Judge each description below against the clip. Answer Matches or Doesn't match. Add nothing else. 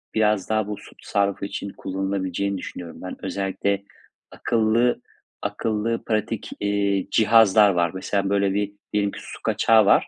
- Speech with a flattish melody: Matches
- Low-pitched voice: Matches